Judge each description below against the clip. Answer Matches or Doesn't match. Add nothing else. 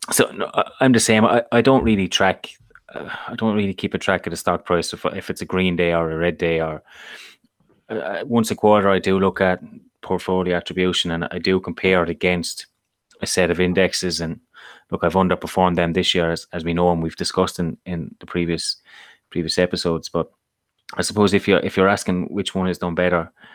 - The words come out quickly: Matches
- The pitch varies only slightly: Matches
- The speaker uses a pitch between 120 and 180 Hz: Doesn't match